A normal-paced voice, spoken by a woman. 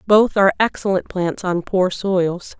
Yes: average, 160 wpm; female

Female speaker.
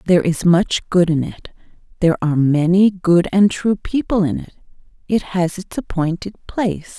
Yes: female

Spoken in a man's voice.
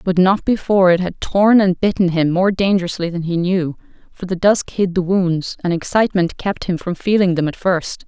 No: female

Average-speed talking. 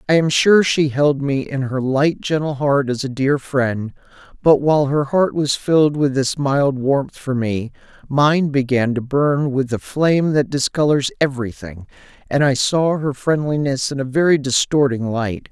Yes: average, 180 wpm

